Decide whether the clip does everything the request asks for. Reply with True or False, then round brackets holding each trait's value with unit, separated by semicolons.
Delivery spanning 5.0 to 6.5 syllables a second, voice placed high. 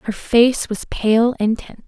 False (4.1 syllables/s; 225 Hz)